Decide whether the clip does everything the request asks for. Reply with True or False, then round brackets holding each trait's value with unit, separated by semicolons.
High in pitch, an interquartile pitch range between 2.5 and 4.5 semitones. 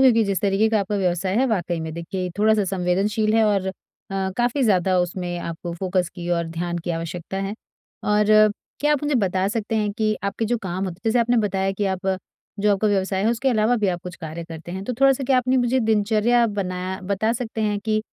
True (200 Hz; 3.5 semitones)